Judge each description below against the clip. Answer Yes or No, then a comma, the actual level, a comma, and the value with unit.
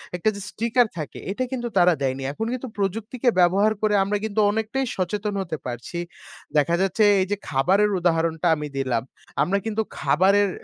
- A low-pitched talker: No, high, 195 Hz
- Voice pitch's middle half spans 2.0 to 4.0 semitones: No, average, 4.8 semitones